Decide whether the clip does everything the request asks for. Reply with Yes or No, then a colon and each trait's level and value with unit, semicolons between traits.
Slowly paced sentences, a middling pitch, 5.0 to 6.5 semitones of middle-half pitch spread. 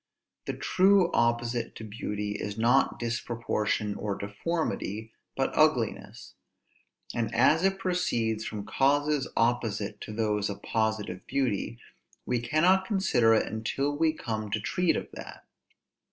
No: slow, 130 wpm; low, 115 Hz; average, 5.3 semitones